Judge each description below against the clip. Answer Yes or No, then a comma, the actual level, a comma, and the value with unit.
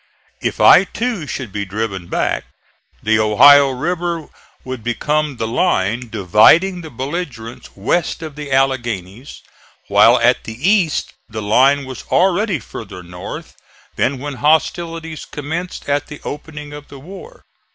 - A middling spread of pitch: No, wide, 6.2 semitones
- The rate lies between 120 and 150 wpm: Yes, average, 140 wpm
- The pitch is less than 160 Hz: Yes, medium, 140 Hz